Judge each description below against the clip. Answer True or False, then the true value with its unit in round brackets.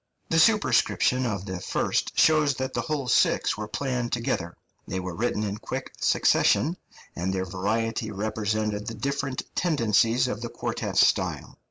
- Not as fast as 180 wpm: True (155 wpm)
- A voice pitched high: False (115 Hz)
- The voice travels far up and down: False (4.2 semitones)